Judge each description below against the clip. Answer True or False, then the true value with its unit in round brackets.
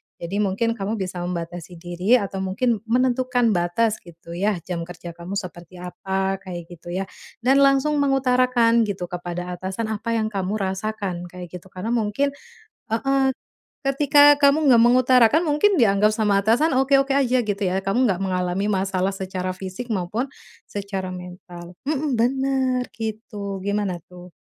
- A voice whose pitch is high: True (205 Hz)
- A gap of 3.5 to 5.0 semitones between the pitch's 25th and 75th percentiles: False (5.4 semitones)